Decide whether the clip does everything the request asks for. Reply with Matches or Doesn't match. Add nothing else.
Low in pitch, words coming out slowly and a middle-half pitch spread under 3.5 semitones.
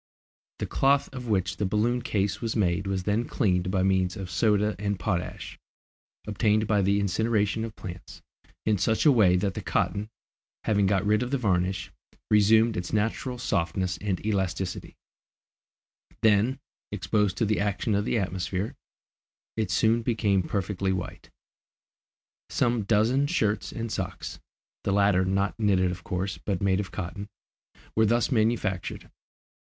Doesn't match